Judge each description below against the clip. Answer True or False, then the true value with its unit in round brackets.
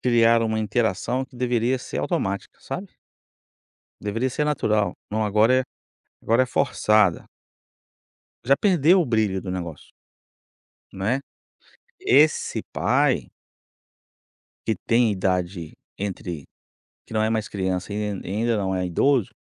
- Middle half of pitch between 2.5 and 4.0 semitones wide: False (4.6 semitones)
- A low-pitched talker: True (110 Hz)